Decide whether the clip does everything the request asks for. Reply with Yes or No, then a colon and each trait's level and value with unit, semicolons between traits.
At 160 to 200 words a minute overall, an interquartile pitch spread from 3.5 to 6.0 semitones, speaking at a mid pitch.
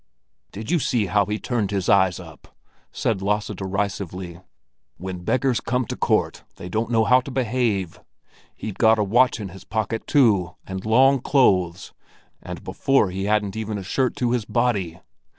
No: average, 170 wpm; average, 4.1 semitones; low, 105 Hz